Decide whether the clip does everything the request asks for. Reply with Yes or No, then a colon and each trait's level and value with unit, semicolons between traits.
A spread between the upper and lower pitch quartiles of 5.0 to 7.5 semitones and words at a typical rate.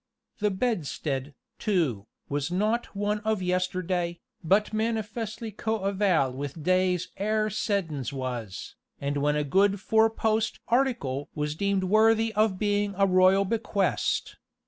No: wide, 5.4 semitones; slow, 125 wpm